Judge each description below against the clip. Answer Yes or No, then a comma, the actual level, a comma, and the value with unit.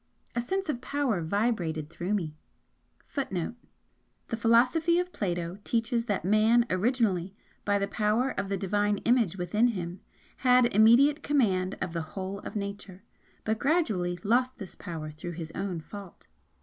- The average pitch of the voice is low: No, high, 205 Hz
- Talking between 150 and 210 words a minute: No, slow, 135 wpm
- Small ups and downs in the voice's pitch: No, average, 4.8 semitones